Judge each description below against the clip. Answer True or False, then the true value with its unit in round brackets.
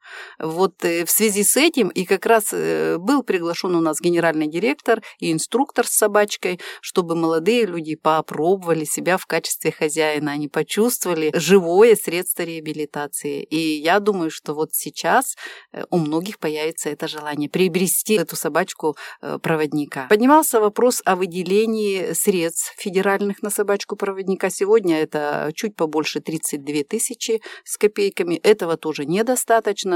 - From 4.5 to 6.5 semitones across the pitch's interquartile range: True (5.2 semitones)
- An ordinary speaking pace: True (130 wpm)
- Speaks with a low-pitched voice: False (180 Hz)